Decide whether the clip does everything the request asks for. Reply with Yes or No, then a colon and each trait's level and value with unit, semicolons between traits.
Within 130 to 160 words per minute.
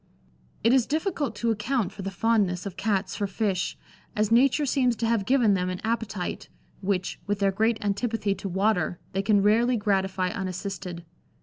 No: average, 175 wpm